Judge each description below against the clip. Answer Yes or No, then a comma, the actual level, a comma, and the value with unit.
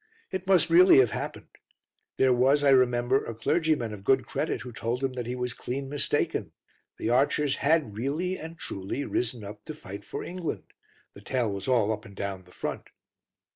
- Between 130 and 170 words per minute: No, average, 190 wpm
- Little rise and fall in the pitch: No, average, 4.8 semitones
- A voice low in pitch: Yes, low, 125 Hz